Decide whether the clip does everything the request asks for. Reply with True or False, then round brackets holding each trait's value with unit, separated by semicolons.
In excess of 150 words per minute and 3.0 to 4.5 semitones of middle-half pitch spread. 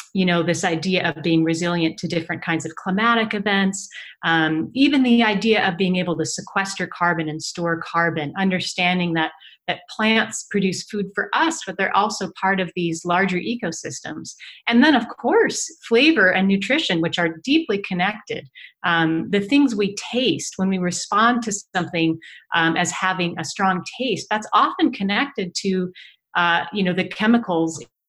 True (165 wpm; 3.7 semitones)